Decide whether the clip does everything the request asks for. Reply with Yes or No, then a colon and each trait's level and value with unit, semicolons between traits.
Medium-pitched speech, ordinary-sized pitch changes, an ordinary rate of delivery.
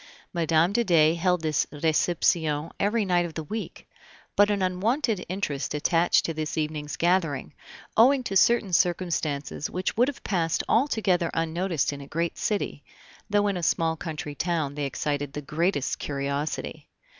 Yes: medium, 170 Hz; average, 4.0 semitones; average, 155 wpm